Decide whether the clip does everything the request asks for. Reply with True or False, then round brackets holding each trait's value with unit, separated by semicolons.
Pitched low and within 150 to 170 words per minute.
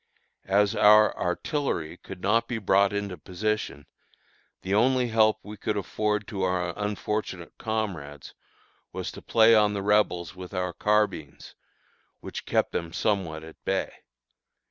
False (105 Hz; 140 wpm)